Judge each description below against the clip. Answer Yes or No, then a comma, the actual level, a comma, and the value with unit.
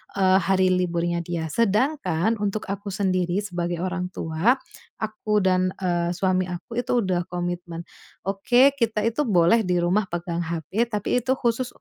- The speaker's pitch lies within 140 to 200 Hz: Yes, medium, 185 Hz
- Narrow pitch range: No, average, 3.6 semitones